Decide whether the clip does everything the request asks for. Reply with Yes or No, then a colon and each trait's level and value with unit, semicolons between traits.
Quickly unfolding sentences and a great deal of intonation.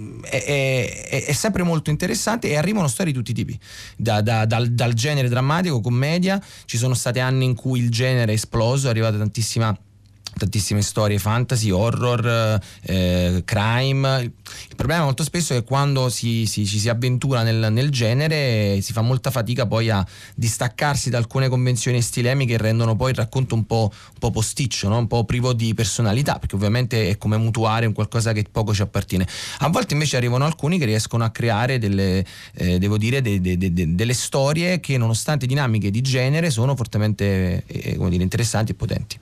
No: fast, 195 wpm; average, 3.6 semitones